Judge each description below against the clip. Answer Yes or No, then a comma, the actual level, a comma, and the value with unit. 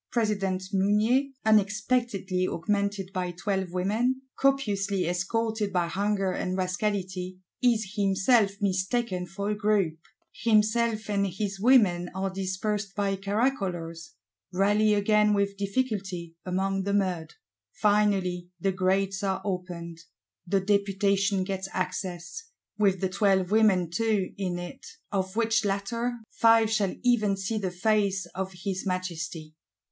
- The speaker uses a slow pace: Yes, slow, 125 wpm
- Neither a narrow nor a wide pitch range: No, narrow, 2.3 semitones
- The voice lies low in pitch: No, high, 195 Hz